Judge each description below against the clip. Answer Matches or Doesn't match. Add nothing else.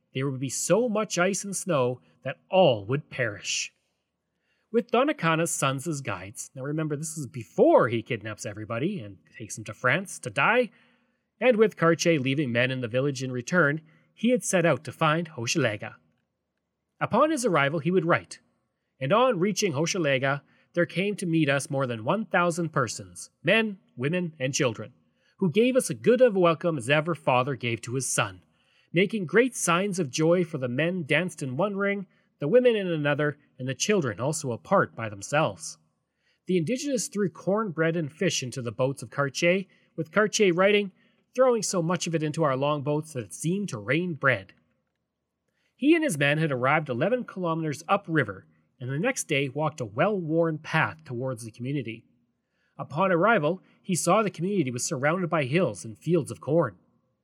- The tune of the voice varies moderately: Doesn't match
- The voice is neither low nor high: Matches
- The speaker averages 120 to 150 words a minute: Doesn't match